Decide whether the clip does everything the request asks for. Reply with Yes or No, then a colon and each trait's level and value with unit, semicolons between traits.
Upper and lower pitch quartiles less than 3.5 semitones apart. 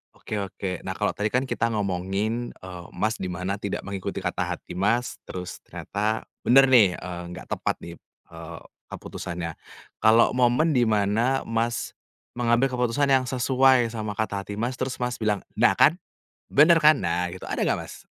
No: average, 4.5 semitones